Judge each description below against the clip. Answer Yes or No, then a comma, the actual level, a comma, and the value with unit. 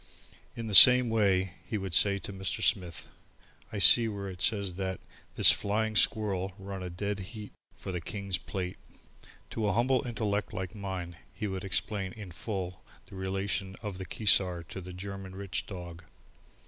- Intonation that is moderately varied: No, narrow, 2.1 semitones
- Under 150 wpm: No, average, 175 wpm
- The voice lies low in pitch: Yes, very low, 95 Hz